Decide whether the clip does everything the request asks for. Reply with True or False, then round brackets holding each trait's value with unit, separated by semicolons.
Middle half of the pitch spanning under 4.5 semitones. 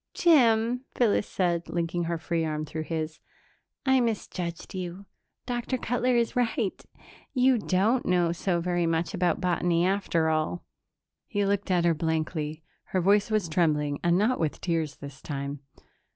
False (4.8 semitones)